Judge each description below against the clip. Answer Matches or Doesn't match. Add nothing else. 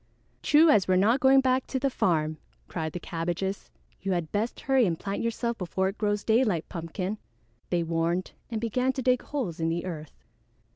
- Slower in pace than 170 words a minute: Doesn't match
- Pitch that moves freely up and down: Matches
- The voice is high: Matches